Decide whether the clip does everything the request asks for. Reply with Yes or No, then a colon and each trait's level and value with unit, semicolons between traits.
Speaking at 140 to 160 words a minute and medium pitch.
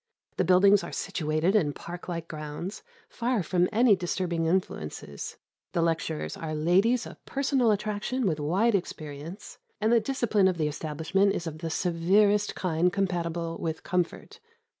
Yes: average, 150 wpm; medium, 180 Hz